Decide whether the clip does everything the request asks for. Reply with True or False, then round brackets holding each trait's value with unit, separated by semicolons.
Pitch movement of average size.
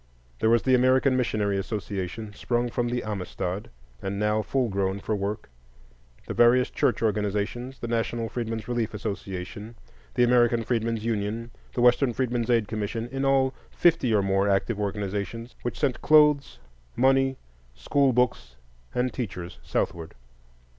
True (3.2 semitones)